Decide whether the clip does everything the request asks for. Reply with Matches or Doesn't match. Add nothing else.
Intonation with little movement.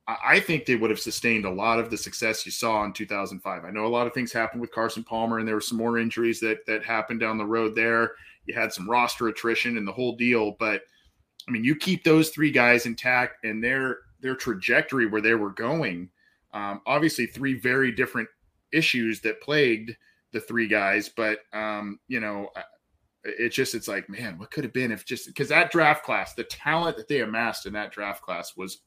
Matches